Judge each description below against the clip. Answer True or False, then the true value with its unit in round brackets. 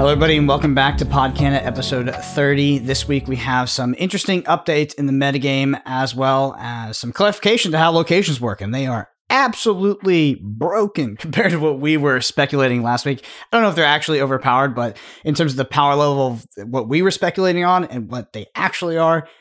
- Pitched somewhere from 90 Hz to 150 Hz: True (140 Hz)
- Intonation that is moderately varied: True (4.1 semitones)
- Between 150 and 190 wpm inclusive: False (205 wpm)